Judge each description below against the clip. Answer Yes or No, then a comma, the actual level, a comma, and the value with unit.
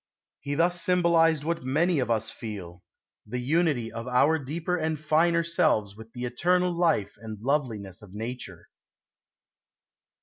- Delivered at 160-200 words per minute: No, average, 140 wpm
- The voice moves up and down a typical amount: No, wide, 6.9 semitones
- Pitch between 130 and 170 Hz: Yes, medium, 140 Hz